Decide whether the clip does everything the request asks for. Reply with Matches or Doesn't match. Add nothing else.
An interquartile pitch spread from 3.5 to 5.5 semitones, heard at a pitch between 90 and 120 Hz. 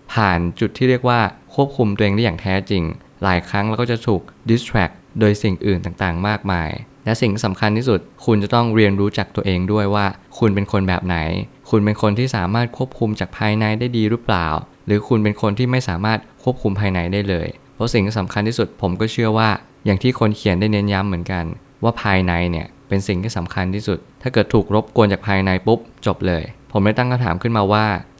Doesn't match